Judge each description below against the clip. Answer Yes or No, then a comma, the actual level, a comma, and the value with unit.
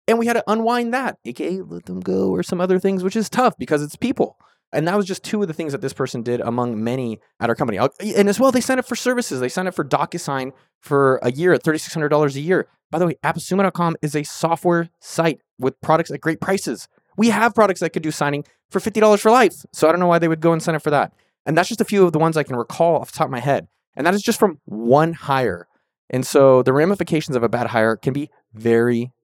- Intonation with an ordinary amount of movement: No, wide, 6.1 semitones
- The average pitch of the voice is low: No, medium, 160 Hz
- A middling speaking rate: No, fast, 265 wpm